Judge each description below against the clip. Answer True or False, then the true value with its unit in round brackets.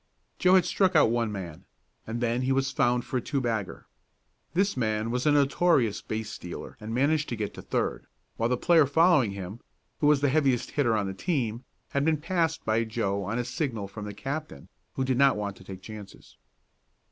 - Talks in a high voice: False (120 Hz)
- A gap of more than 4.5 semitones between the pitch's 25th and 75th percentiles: True (5.1 semitones)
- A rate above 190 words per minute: True (205 wpm)